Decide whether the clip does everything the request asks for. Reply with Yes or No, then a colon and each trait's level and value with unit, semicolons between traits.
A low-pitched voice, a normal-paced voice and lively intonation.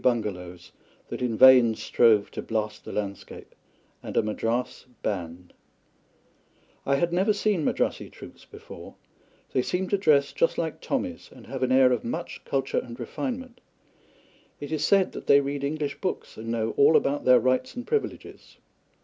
Yes: low, 130 Hz; average, 165 wpm; wide, 6.7 semitones